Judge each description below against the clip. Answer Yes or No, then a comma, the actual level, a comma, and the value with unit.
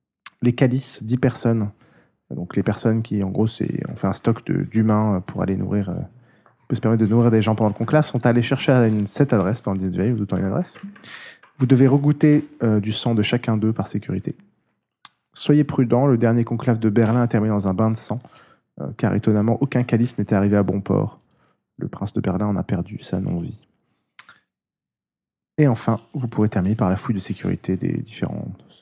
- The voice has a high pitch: No, low, 115 Hz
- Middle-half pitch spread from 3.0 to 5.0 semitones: Yes, average, 3.3 semitones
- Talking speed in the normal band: Yes, average, 200 wpm